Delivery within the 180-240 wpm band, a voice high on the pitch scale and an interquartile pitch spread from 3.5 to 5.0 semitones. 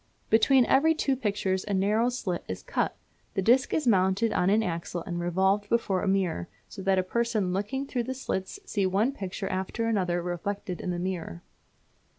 Yes: average, 185 wpm; high, 195 Hz; average, 3.9 semitones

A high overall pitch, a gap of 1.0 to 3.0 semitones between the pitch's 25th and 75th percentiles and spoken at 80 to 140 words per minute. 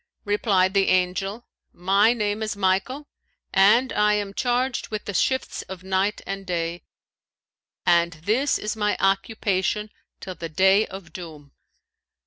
Yes: high, 195 Hz; narrow, 2.4 semitones; slow, 135 wpm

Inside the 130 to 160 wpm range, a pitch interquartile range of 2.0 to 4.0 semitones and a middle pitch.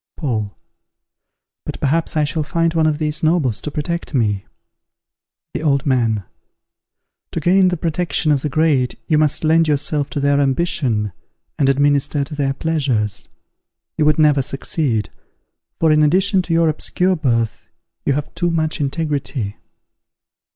Yes: average, 150 wpm; average, 3.1 semitones; medium, 150 Hz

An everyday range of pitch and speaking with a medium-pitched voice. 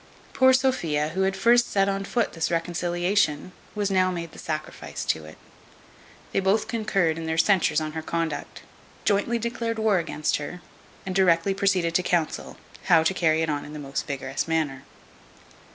Yes: average, 3.8 semitones; medium, 175 Hz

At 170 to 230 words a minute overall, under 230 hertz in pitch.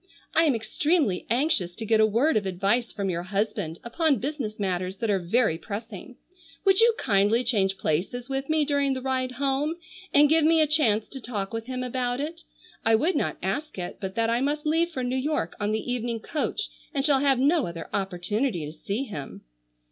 No: fast, 205 wpm; high, 245 Hz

